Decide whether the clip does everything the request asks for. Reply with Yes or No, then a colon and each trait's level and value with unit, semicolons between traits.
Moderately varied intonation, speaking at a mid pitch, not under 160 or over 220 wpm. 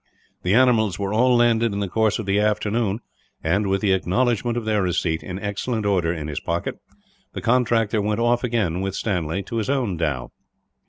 No: average, 3.7 semitones; low, 105 Hz; average, 195 wpm